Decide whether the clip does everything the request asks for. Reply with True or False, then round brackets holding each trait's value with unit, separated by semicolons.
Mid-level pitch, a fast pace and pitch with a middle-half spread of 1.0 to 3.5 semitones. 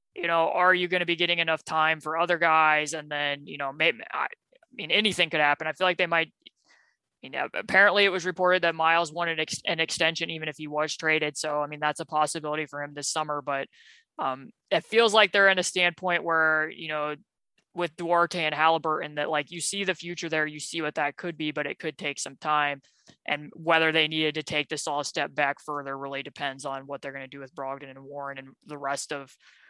True (155 Hz; 235 wpm; 2.7 semitones)